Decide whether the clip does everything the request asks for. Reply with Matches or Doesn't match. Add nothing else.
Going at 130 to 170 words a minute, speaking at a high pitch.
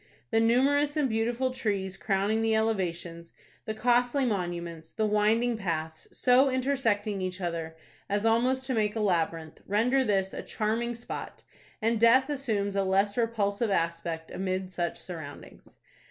Matches